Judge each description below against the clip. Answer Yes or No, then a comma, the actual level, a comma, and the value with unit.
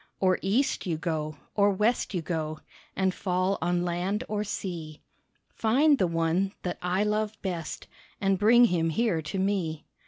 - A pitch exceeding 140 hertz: Yes, medium, 185 Hz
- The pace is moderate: Yes, average, 160 wpm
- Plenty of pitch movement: No, average, 3.8 semitones